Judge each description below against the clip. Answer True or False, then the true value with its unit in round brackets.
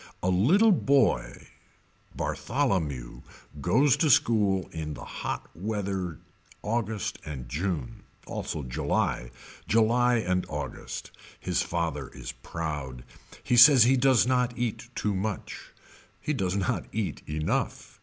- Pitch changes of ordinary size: False (7.1 semitones)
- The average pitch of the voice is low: True (100 Hz)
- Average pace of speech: False (120 wpm)